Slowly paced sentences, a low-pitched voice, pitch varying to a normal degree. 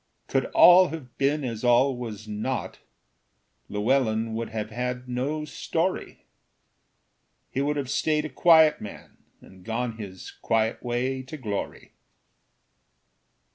Yes: slow, 125 wpm; low, 125 Hz; average, 4.3 semitones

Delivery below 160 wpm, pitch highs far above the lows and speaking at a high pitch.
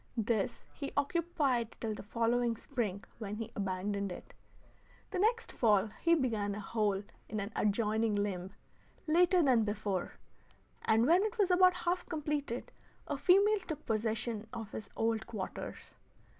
Yes: average, 145 wpm; wide, 6.7 semitones; high, 230 Hz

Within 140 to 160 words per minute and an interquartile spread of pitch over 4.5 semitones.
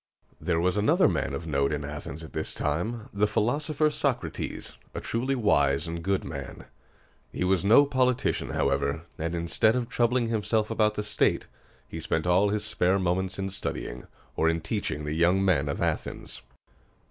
No: average, 170 wpm; wide, 5.6 semitones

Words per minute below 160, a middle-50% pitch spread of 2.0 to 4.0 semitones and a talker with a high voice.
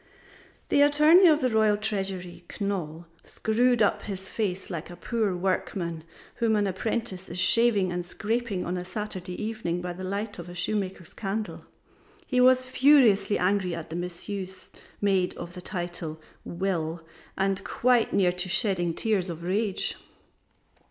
Yes: average, 150 wpm; average, 3.5 semitones; high, 195 Hz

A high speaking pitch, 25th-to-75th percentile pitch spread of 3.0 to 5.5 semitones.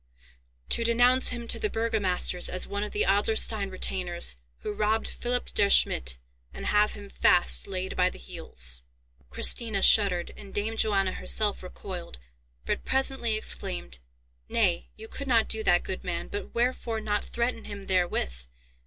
Yes: high, 205 Hz; average, 3.6 semitones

